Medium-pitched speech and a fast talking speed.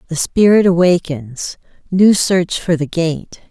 No: medium, 170 Hz; slow, 135 wpm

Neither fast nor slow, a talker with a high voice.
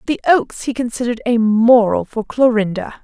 Yes: average, 160 wpm; high, 240 Hz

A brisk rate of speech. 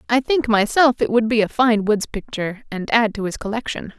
Yes: fast, 225 wpm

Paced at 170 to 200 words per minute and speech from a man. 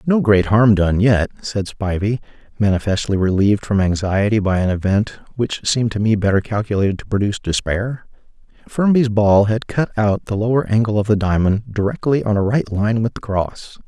Yes: average, 180 wpm; male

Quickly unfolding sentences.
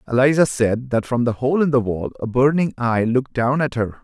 Yes: fast, 240 wpm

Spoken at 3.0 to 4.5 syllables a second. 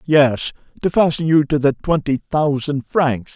Yes: 4.2 syllables/s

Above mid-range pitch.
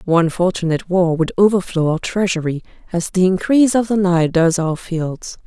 No: medium, 180 Hz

